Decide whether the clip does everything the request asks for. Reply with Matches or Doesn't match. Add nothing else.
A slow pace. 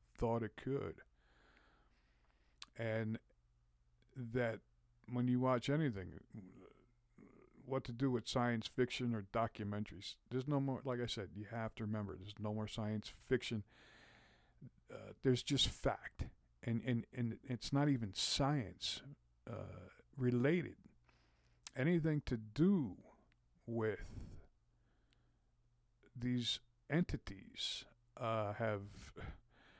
Matches